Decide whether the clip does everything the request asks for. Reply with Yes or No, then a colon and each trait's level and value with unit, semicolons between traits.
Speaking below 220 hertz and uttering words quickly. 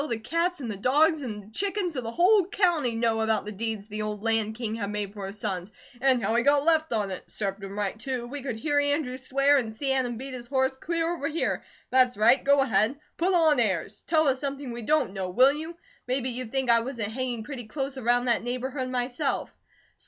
No: very high, 250 Hz; fast, 230 wpm